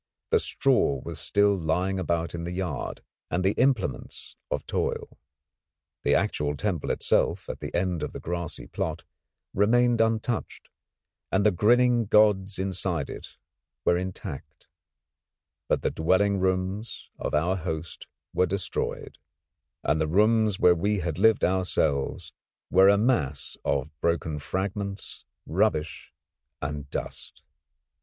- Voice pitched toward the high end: No, very low, 95 Hz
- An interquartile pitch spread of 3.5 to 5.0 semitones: Yes, average, 3.9 semitones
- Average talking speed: No, slow, 130 wpm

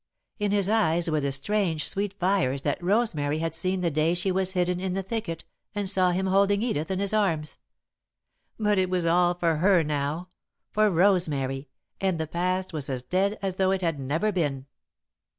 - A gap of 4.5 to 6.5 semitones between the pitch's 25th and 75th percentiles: No, average, 3.6 semitones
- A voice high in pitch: No, medium, 180 Hz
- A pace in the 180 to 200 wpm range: Yes, average, 190 wpm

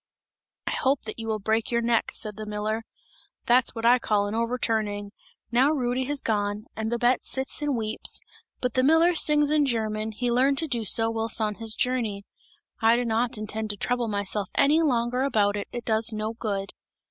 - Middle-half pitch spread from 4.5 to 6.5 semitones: No, average, 2.8 semitones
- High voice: Yes, high, 230 Hz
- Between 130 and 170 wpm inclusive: No, average, 195 wpm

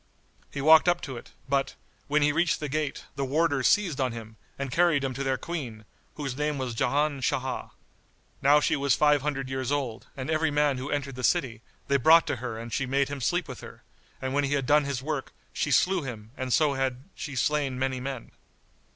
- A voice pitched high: No, medium, 140 Hz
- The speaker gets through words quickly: Yes, fast, 220 wpm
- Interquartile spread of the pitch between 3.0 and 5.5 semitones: No, narrow, 2.4 semitones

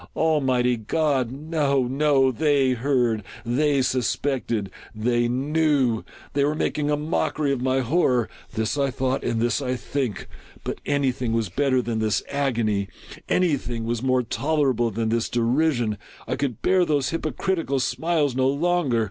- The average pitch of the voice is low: Yes, low, 130 Hz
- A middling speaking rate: Yes, average, 175 wpm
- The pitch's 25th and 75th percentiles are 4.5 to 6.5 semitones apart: No, average, 3.5 semitones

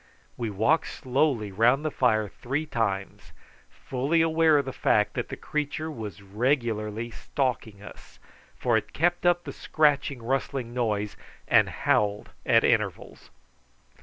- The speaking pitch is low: Yes, low, 125 Hz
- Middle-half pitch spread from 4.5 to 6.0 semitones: Yes, wide, 5.5 semitones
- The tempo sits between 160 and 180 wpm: No, slow, 135 wpm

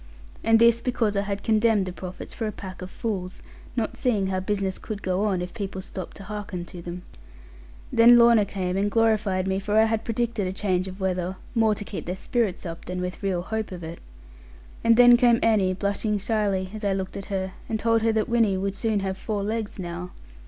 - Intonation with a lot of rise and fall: No, average, 2.9 semitones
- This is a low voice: No, high, 200 Hz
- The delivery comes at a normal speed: No, fast, 215 wpm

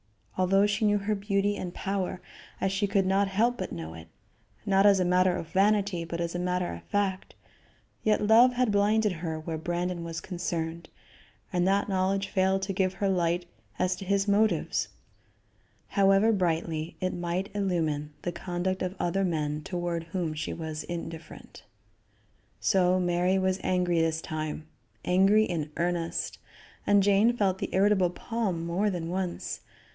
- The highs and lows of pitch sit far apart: No, average, 2.7 semitones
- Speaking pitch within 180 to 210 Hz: Yes, medium, 185 Hz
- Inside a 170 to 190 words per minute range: No, average, 160 wpm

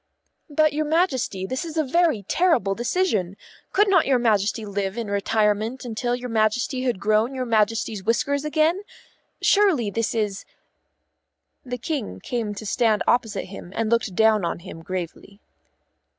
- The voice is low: No, high, 230 Hz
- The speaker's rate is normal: Yes, average, 160 wpm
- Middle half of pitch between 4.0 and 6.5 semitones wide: Yes, average, 5.0 semitones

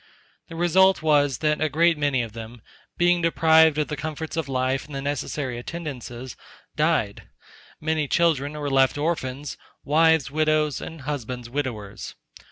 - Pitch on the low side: No, medium, 145 Hz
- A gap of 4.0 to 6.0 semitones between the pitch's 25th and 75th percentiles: No, average, 3.4 semitones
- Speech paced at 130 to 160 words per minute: Yes, average, 150 wpm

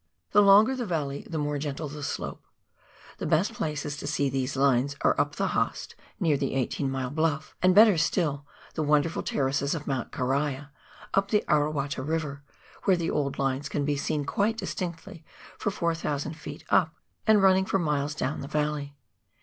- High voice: No, medium, 150 Hz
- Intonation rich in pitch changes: No, average, 3.2 semitones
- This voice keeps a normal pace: Yes, average, 180 wpm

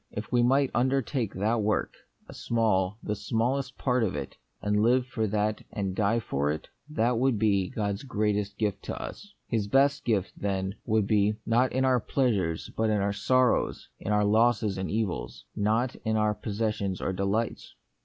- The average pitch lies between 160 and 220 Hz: No, low, 110 Hz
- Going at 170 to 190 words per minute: Yes, average, 185 wpm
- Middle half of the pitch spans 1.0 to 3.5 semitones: Yes, average, 3.1 semitones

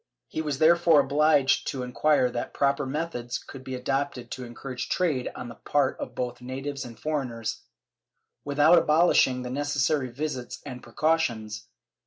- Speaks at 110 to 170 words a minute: Yes, average, 150 wpm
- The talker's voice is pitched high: No, low, 135 Hz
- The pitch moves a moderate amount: Yes, average, 3.3 semitones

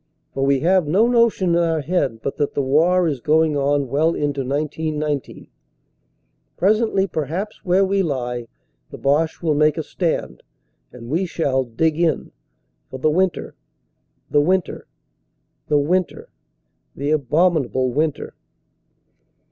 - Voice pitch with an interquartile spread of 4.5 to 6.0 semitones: No, average, 4.0 semitones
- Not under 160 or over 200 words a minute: No, slow, 135 wpm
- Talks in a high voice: No, medium, 155 Hz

